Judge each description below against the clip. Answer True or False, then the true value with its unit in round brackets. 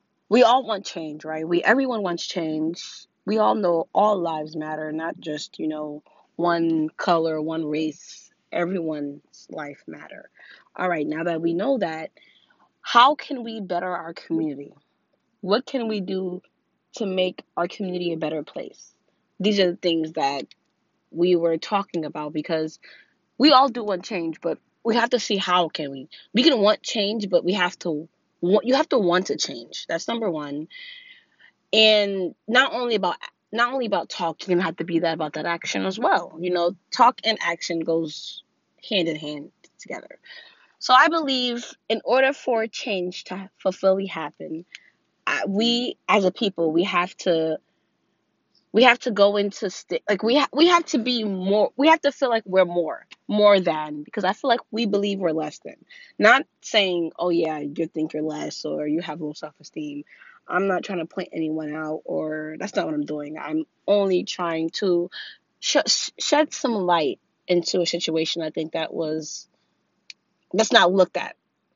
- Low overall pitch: False (180 Hz)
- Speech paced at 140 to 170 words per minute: False (180 wpm)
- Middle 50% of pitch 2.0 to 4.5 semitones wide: False (5.3 semitones)